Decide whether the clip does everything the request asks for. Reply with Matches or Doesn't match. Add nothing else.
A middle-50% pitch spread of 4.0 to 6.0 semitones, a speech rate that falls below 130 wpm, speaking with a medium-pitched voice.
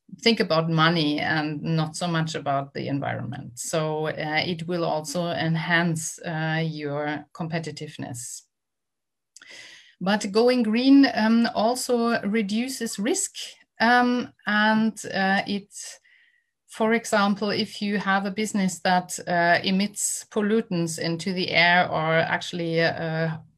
Matches